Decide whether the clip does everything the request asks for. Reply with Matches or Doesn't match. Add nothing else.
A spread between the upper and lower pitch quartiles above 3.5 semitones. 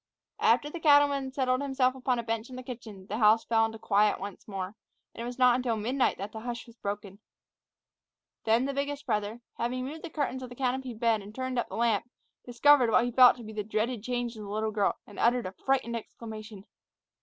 Doesn't match